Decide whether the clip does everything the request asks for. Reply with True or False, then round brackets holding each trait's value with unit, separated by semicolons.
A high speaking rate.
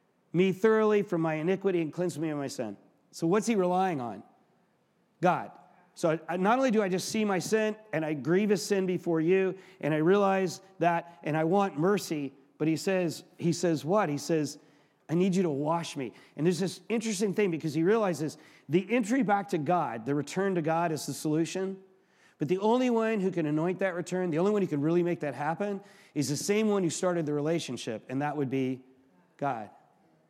True (215 wpm)